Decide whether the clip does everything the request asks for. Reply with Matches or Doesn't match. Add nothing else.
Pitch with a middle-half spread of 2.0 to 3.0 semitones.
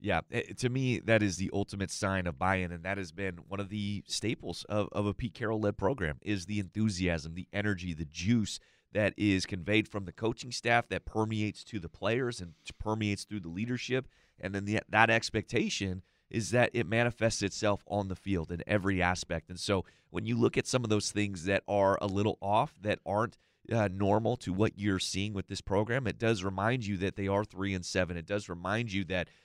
Matches